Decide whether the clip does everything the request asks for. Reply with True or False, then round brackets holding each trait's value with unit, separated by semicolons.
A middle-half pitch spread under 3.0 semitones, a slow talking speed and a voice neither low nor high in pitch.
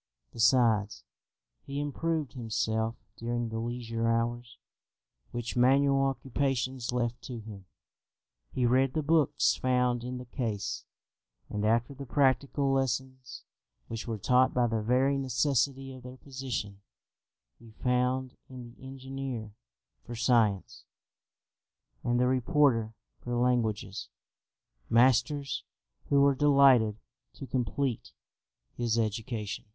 False (2.6 semitones; 115 wpm; 125 Hz)